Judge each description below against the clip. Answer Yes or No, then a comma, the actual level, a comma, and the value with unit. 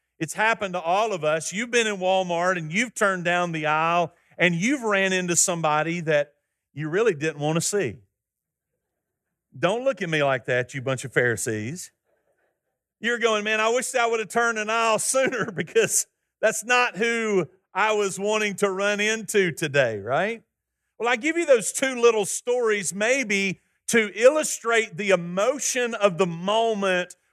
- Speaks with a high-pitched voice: Yes, high, 200 Hz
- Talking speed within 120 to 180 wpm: Yes, average, 170 wpm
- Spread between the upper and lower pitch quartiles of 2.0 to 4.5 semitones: No, average, 5.2 semitones